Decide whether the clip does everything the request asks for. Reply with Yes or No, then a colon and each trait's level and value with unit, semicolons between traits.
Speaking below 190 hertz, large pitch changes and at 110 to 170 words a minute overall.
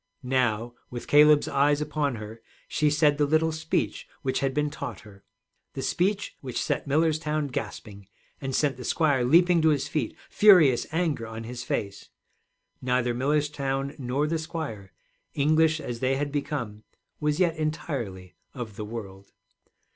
No: medium, 140 Hz; average, 4.2 semitones; average, 155 wpm